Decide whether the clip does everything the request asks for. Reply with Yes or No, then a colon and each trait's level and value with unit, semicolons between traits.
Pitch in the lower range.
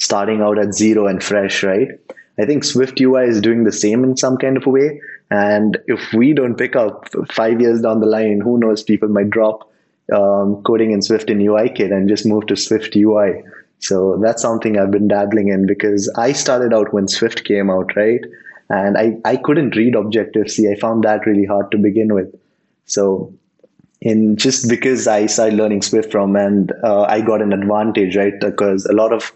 Yes: low, 105 Hz